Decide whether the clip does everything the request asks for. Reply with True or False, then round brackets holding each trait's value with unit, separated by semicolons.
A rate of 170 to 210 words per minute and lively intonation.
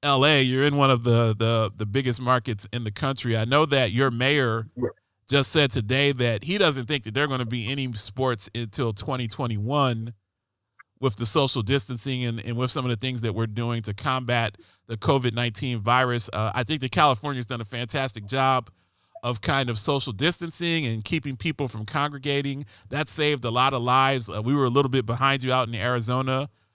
False (205 wpm; 3.0 semitones)